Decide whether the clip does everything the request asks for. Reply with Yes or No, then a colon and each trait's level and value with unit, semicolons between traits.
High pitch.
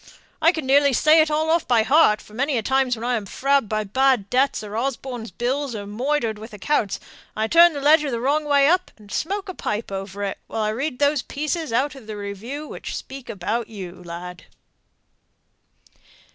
Yes: very high, 250 Hz